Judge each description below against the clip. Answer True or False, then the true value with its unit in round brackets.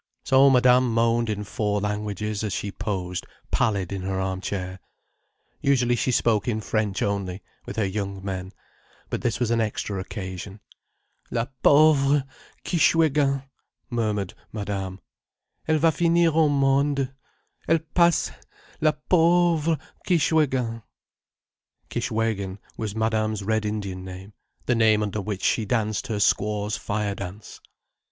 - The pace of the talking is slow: True (130 wpm)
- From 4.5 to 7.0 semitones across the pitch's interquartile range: True (5.1 semitones)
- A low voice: True (110 Hz)